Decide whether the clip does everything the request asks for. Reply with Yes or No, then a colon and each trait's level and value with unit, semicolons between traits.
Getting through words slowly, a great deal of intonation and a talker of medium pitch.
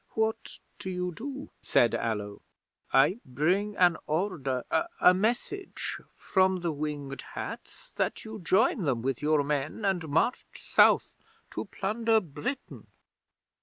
Yes: slow, 130 wpm; wide, 6.9 semitones; medium, 180 Hz